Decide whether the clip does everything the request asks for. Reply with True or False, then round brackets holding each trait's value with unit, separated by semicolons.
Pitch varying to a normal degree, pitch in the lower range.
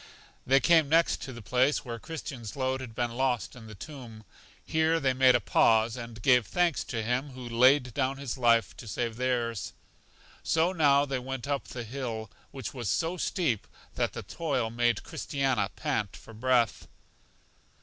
True (3.0 semitones; 125 Hz)